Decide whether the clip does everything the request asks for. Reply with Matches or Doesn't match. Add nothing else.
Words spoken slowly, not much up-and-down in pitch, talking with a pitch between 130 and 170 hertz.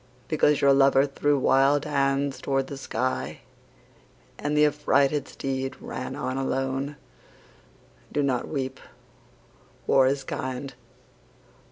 Matches